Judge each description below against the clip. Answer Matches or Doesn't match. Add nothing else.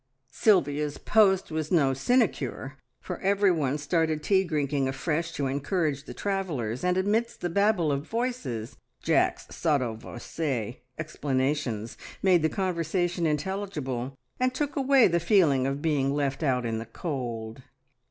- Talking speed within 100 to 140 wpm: Matches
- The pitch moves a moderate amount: Doesn't match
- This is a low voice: Doesn't match